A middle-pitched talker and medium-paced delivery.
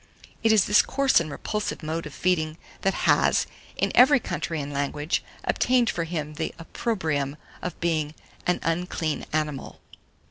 Yes: medium, 165 Hz; average, 150 wpm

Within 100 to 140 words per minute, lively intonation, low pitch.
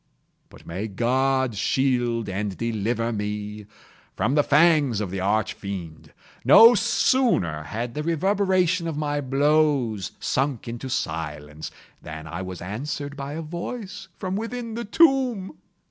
Yes: slow, 135 wpm; wide, 8.2 semitones; low, 130 Hz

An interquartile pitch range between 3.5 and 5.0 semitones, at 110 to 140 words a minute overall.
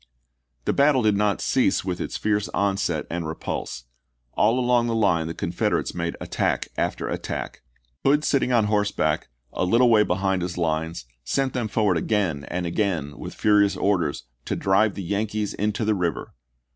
No: average, 3.9 semitones; average, 170 wpm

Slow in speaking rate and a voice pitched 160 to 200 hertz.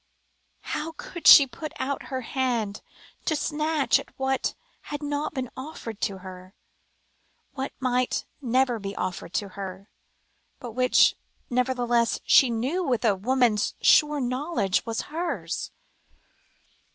No: slow, 130 wpm; very high, 255 Hz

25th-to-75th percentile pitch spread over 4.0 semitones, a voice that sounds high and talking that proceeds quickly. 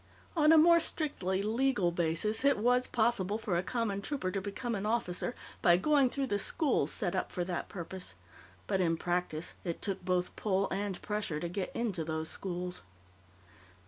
No: average, 5.0 semitones; high, 195 Hz; average, 175 wpm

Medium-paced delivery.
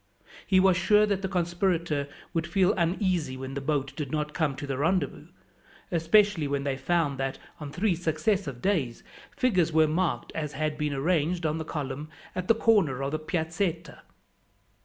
Yes: average, 175 wpm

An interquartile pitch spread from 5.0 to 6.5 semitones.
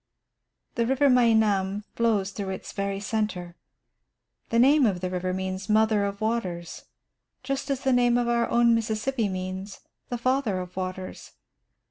No: average, 4.0 semitones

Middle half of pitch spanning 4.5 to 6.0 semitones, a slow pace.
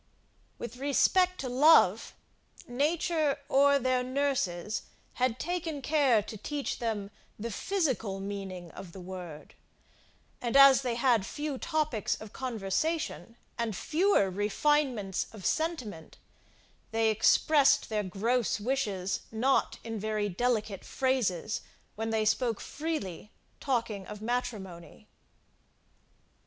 Yes: average, 5.2 semitones; slow, 115 wpm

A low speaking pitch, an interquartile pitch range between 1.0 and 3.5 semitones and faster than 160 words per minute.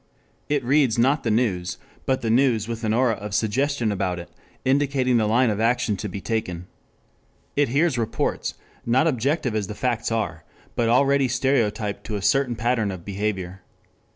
No: low, 115 Hz; average, 3.9 semitones; average, 175 wpm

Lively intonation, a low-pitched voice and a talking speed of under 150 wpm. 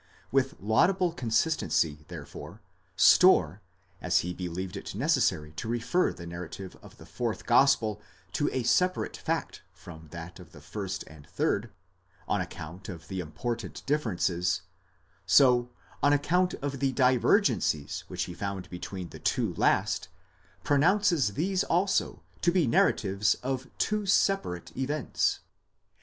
Yes: wide, 8.2 semitones; low, 110 Hz; slow, 135 wpm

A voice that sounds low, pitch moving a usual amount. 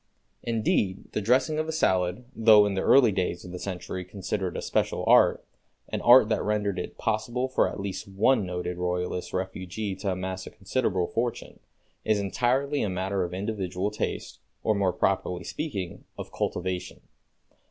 Yes: low, 100 Hz; average, 3.3 semitones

